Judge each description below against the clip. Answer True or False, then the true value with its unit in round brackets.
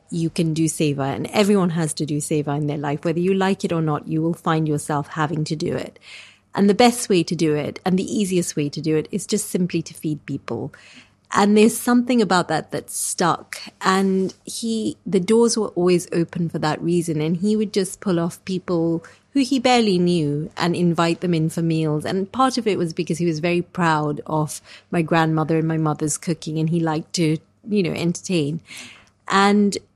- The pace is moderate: False (210 wpm)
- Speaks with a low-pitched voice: False (170 Hz)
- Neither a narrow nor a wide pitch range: True (3.6 semitones)